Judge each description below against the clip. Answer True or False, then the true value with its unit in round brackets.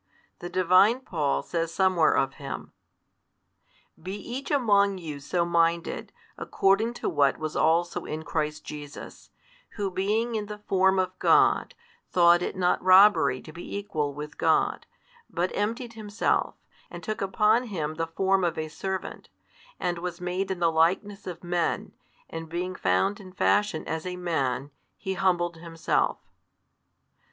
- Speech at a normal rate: True (150 wpm)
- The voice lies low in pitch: False (180 Hz)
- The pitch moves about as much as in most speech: True (3.4 semitones)